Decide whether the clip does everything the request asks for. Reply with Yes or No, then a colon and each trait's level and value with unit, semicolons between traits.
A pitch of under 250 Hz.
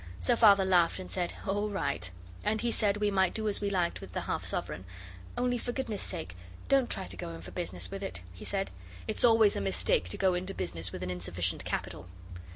Yes: high, 190 Hz